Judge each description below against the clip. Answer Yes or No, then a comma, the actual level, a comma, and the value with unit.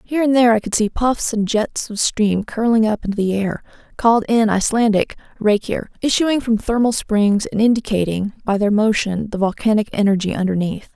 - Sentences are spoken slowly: No, average, 180 wpm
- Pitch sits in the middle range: No, high, 215 Hz